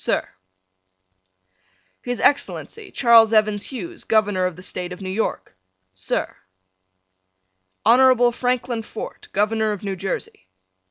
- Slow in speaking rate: Yes, slow, 115 wpm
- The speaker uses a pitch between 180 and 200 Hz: No, high, 220 Hz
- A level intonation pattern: No, average, 4.1 semitones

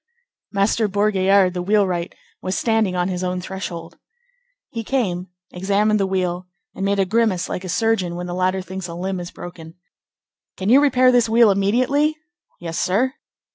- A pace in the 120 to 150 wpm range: No, average, 170 wpm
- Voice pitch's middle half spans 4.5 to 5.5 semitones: No, average, 3.5 semitones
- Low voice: No, high, 190 Hz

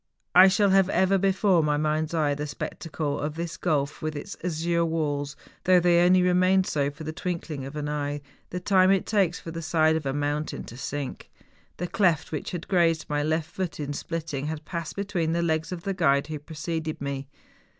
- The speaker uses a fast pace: Yes, fast, 215 wpm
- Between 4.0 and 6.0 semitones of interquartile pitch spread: No, average, 3.2 semitones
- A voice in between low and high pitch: Yes, medium, 160 Hz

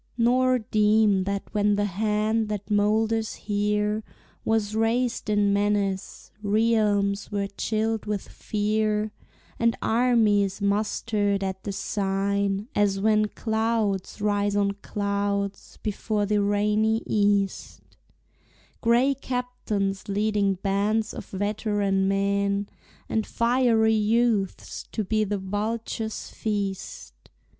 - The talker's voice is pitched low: No, high, 210 Hz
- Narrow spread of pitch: Yes, narrow, 1.6 semitones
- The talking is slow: Yes, slow, 105 wpm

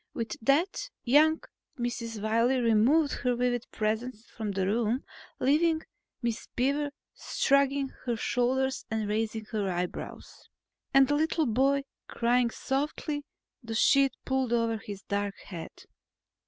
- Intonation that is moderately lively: Yes, average, 3.8 semitones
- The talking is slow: Yes, slow, 125 wpm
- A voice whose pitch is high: Yes, high, 245 Hz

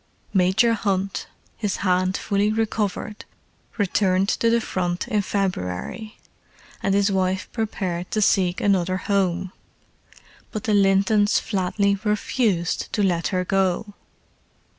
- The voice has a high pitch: Yes, high, 195 Hz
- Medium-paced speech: No, slow, 120 wpm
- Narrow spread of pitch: Yes, narrow, 2.2 semitones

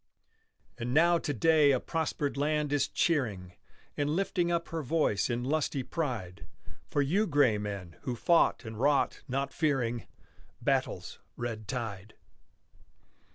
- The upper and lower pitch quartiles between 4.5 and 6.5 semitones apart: Yes, wide, 5.4 semitones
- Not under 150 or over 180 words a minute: No, slow, 135 wpm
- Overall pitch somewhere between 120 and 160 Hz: Yes, medium, 140 Hz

